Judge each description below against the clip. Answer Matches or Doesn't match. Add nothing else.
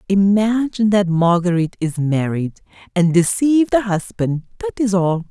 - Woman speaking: Matches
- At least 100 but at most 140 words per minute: Matches